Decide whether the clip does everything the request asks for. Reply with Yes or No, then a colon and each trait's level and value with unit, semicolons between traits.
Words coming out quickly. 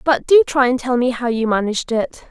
Yes: fast, 260 wpm